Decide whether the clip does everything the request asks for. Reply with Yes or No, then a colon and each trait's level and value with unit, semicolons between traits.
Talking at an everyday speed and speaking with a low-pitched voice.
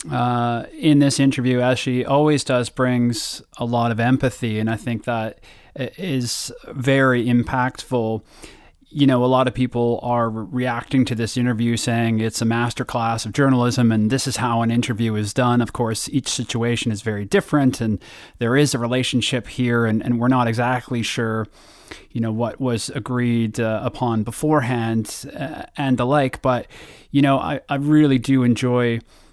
Yes: average, 175 wpm; low, 120 Hz